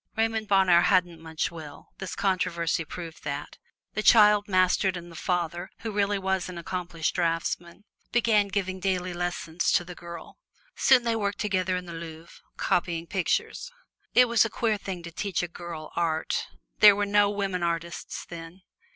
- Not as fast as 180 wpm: Yes, average, 170 wpm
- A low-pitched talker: No, medium, 180 Hz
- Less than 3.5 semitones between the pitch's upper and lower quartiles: Yes, average, 3.0 semitones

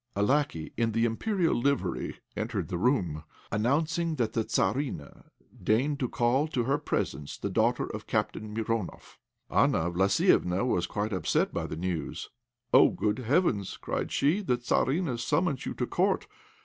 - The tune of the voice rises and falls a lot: Yes, wide, 6.0 semitones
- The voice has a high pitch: No, low, 115 Hz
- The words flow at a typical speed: Yes, average, 155 wpm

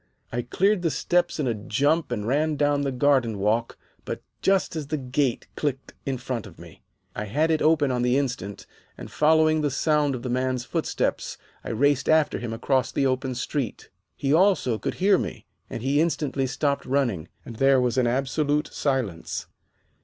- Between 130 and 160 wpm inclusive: No, average, 185 wpm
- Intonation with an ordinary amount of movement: Yes, average, 3.4 semitones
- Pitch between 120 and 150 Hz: Yes, low, 135 Hz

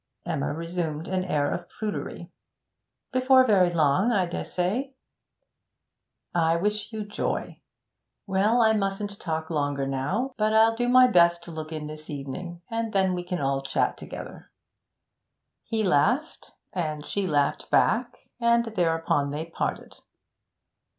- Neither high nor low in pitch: Yes, medium, 180 Hz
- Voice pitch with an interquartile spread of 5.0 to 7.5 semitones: Yes, wide, 5.6 semitones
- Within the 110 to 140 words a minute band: Yes, slow, 135 wpm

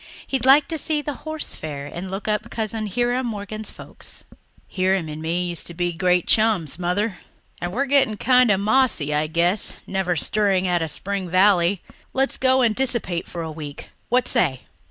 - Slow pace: No, average, 185 wpm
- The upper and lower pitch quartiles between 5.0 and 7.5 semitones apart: Yes, wide, 5.5 semitones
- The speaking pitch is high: Yes, high, 195 Hz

